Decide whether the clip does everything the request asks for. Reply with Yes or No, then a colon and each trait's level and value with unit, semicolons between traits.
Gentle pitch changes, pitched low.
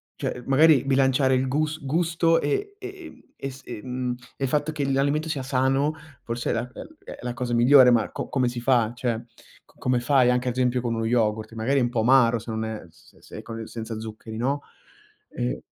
No: average, 3.0 semitones; low, 125 Hz